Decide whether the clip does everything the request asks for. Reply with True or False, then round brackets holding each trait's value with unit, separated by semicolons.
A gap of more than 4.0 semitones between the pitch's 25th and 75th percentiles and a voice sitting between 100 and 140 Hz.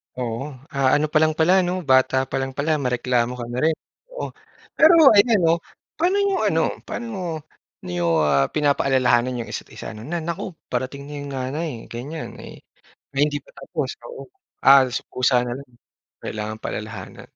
True (4.5 semitones; 135 Hz)